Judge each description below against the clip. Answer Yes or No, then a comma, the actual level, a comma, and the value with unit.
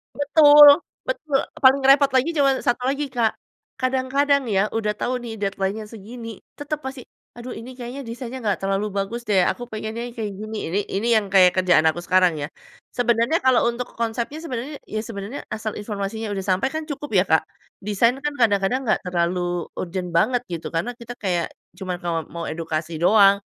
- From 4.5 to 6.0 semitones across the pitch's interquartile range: Yes, average, 5.0 semitones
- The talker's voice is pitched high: Yes, high, 225 Hz